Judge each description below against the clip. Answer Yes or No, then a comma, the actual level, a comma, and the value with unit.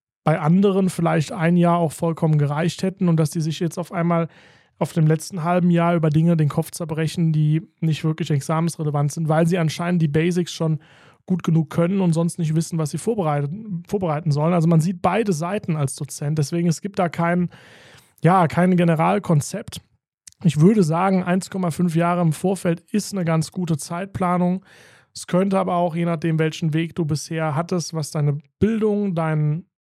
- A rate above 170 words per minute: Yes, average, 185 wpm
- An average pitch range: No, narrow, 2.0 semitones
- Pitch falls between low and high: Yes, medium, 170 Hz